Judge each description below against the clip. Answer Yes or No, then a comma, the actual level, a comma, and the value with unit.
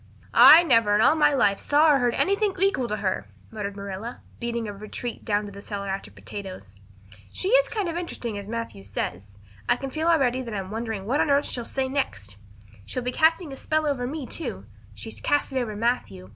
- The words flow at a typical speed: No, fast, 215 wpm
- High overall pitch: Yes, high, 235 Hz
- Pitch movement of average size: No, wide, 6.3 semitones